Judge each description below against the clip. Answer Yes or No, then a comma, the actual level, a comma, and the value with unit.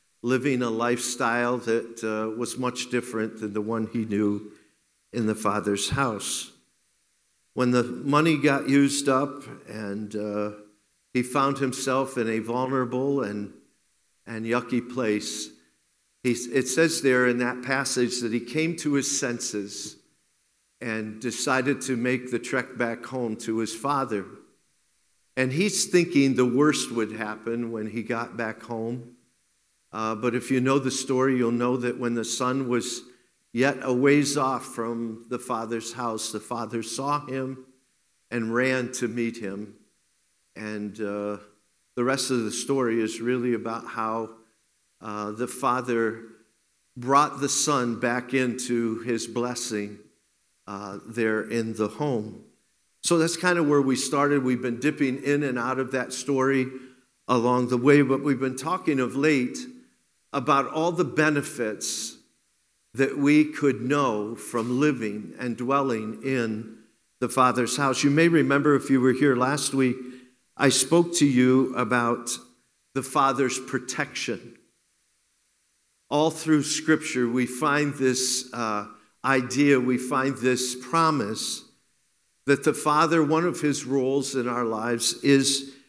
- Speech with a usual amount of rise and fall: Yes, average, 3.1 semitones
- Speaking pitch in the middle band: No, low, 125 Hz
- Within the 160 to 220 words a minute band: No, average, 145 wpm